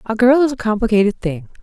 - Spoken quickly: Yes, fast, 220 wpm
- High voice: Yes, high, 225 Hz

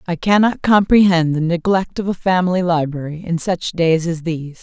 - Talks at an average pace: Yes, average, 180 wpm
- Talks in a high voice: No, medium, 175 Hz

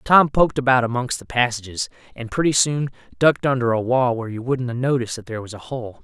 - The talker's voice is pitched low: Yes, low, 125 Hz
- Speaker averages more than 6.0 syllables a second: Yes, 6.5 syllables/s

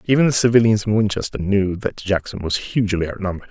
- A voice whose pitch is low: Yes, low, 105 Hz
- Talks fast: No, average, 190 wpm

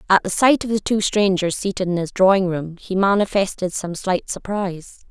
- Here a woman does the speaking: Yes, female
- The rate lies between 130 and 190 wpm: No, average, 200 wpm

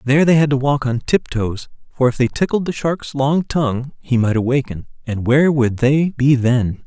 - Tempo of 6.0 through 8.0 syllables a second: No, 5.0 syllables/s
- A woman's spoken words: No, male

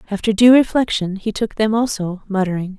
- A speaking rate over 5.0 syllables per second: Yes, 5.6 syllables/s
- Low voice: No, high, 210 Hz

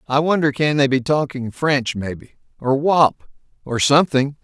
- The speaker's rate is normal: Yes, average, 160 wpm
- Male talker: Yes, male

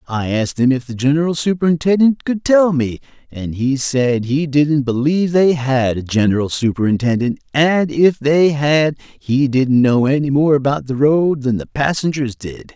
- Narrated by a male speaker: Yes, male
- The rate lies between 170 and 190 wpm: Yes, average, 175 wpm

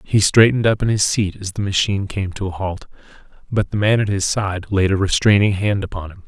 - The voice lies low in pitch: Yes, low, 100 Hz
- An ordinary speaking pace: No, fast, 230 wpm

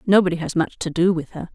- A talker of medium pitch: Yes, medium, 170 Hz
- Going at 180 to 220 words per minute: No, fast, 270 wpm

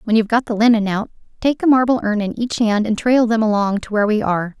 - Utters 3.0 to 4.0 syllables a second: No, 6.5 syllables/s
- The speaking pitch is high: Yes, high, 220 Hz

